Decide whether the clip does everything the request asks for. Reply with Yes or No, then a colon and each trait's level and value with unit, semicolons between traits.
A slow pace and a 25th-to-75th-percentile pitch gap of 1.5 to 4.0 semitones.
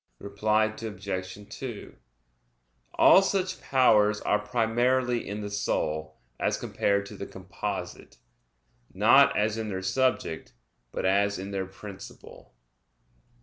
Yes: slow, 115 wpm; average, 3.0 semitones